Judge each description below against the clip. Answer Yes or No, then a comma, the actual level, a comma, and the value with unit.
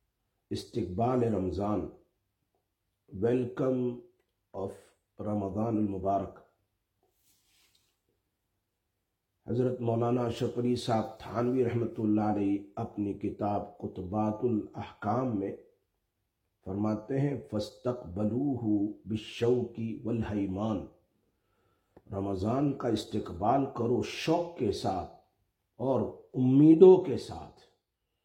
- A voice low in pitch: Yes, low, 110 Hz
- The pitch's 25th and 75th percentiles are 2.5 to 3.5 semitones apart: Yes, average, 3.2 semitones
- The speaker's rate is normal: No, slow, 75 wpm